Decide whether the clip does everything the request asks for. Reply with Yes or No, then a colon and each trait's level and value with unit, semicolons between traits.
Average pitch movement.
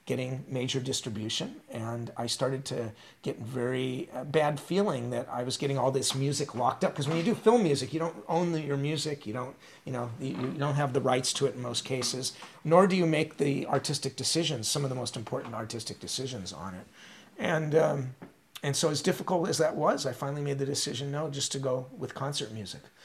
Yes: average, 3.4 semitones